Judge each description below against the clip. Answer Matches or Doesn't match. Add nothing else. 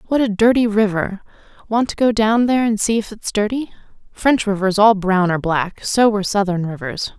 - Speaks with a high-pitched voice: Matches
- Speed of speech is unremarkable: Matches